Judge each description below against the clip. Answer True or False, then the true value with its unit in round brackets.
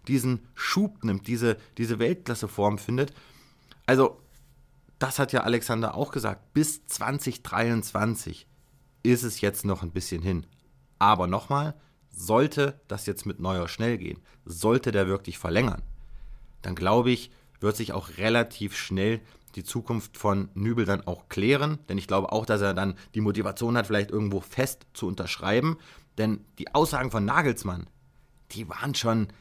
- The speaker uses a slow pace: False (150 wpm)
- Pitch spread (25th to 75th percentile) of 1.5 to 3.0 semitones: False (4.7 semitones)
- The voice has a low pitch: True (110 Hz)